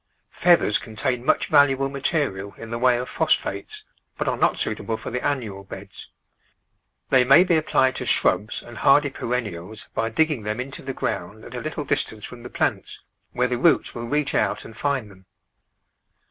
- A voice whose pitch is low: Yes, low, 125 Hz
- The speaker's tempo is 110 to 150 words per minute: No, average, 185 wpm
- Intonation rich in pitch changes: No, average, 4.1 semitones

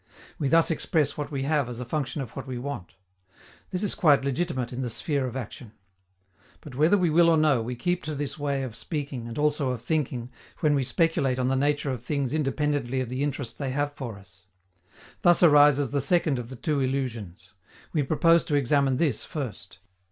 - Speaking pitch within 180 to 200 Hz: No, medium, 140 Hz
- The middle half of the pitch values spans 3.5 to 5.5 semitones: No, average, 3.1 semitones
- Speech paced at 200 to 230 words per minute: Yes, fast, 205 wpm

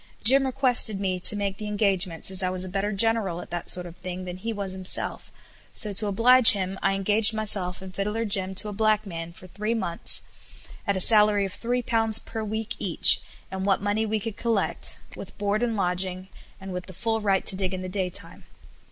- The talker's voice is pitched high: Yes, high, 200 Hz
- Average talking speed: No, fast, 220 wpm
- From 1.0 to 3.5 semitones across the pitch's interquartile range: Yes, average, 2.8 semitones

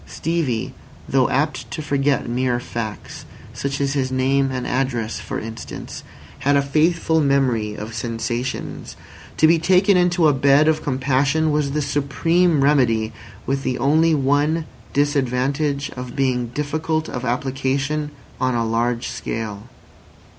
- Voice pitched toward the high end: No, low, 135 Hz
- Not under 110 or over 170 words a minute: Yes, average, 140 wpm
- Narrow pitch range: No, average, 3.2 semitones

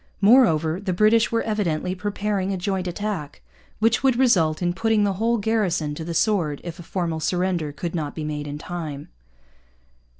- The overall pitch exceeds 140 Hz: Yes, medium, 185 Hz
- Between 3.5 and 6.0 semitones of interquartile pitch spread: Yes, average, 4.8 semitones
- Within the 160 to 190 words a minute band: Yes, average, 175 wpm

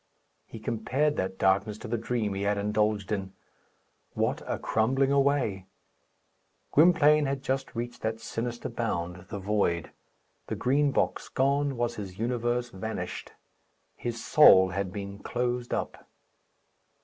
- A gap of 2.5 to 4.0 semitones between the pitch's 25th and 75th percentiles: No, average, 4.6 semitones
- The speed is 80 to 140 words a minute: Yes, slow, 135 wpm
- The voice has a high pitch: No, low, 115 Hz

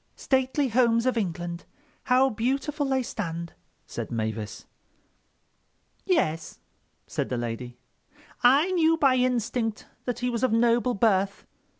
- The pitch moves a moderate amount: No, wide, 6.9 semitones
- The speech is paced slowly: Yes, slow, 115 wpm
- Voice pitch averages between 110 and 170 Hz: No, high, 240 Hz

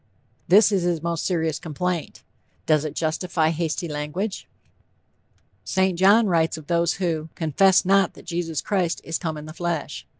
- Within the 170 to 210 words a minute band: No, average, 160 wpm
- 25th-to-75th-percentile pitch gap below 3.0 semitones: Yes, narrow, 2.6 semitones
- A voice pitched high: No, medium, 170 Hz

